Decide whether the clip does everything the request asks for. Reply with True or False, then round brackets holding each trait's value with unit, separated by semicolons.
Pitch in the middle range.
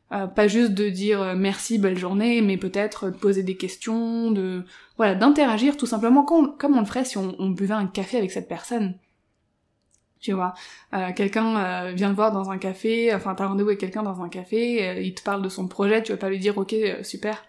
False (200 Hz)